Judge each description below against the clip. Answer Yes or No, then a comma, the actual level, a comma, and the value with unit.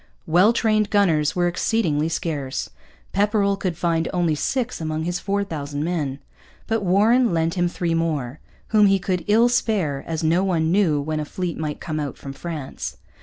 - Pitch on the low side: No, medium, 170 Hz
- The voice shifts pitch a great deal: No, average, 4.4 semitones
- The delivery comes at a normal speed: Yes, average, 175 wpm